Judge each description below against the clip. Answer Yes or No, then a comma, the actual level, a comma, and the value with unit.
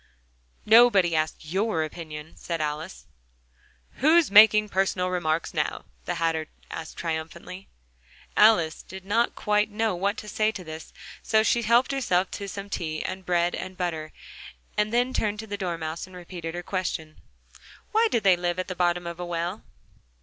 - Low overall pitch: No, medium, 185 Hz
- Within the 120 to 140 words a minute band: No, average, 165 wpm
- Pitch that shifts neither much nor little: Yes, average, 4.0 semitones